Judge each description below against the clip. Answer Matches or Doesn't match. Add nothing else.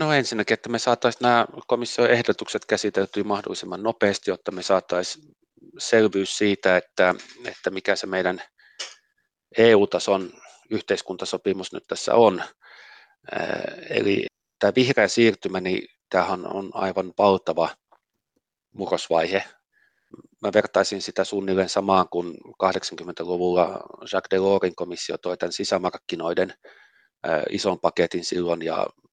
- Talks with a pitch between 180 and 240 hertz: Doesn't match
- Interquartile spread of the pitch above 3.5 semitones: Doesn't match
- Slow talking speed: Doesn't match